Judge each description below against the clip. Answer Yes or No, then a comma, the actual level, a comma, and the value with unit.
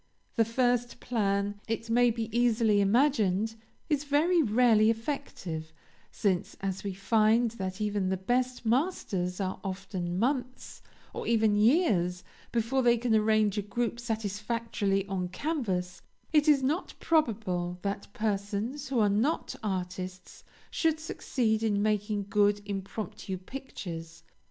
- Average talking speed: No, slow, 130 wpm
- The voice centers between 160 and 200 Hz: No, high, 215 Hz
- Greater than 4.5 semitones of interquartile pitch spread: No, average, 3.7 semitones